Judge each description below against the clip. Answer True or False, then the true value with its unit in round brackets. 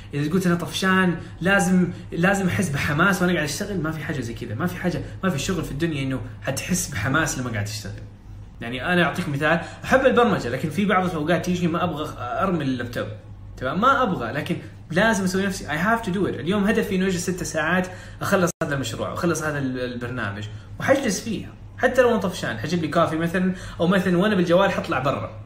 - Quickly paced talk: True (200 wpm)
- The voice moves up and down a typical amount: False (6.5 semitones)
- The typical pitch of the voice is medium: True (165 Hz)